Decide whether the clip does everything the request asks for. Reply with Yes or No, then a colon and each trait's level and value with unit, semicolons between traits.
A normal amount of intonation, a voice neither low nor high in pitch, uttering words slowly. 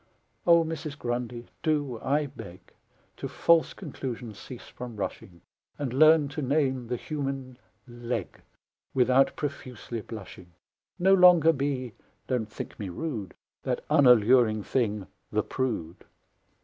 No: average, 4.0 semitones; low, 130 Hz; slow, 125 wpm